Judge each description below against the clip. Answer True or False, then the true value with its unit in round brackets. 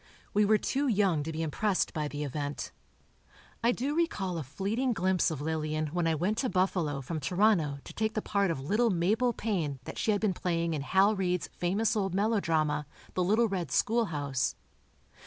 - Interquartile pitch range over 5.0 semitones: True (5.6 semitones)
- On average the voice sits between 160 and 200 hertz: True (185 Hz)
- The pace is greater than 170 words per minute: True (190 wpm)